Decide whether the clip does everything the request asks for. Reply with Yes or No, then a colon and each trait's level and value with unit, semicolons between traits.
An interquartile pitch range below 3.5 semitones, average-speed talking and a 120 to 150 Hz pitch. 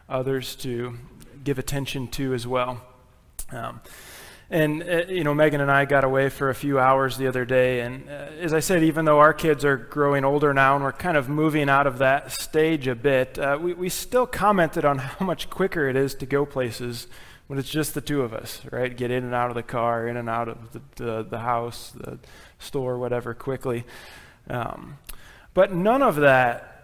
No: average, 2.9 semitones; fast, 210 wpm; low, 135 Hz